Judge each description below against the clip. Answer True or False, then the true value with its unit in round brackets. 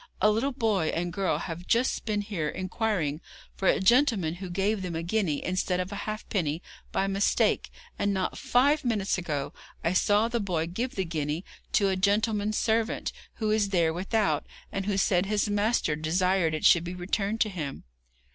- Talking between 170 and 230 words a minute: True (185 wpm)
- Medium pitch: False (195 Hz)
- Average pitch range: True (3.6 semitones)